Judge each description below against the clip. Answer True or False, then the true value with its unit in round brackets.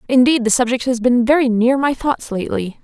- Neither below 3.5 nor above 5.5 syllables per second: False (5.7 syllables/s)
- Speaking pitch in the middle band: False (245 Hz)